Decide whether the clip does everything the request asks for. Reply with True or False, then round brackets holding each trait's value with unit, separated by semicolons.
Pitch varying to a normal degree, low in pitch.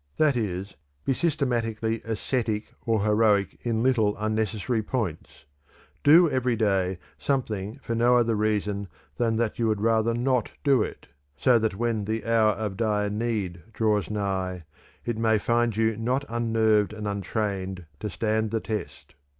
False (2.2 semitones; 110 Hz)